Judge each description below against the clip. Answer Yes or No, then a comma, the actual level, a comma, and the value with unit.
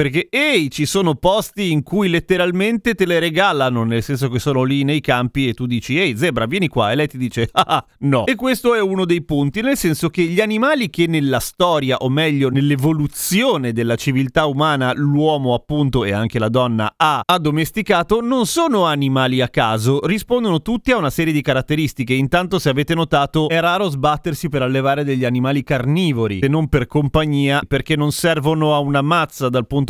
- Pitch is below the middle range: No, medium, 150 Hz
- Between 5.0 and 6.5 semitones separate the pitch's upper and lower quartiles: No, average, 4.6 semitones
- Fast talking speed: Yes, fast, 190 wpm